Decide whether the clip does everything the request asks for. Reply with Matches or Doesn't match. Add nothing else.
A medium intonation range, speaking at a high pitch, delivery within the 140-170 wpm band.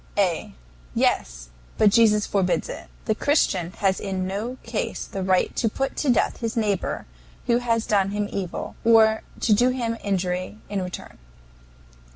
Matches